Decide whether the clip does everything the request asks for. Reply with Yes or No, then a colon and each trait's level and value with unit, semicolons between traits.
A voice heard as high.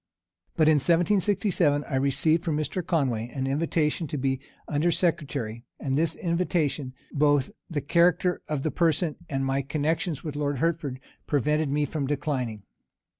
No: medium, 150 Hz